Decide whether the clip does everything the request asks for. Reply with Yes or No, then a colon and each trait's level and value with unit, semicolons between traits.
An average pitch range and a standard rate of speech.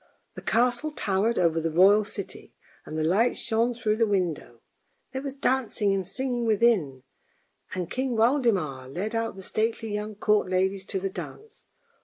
Yes: average, 4.2 semitones; average, 165 wpm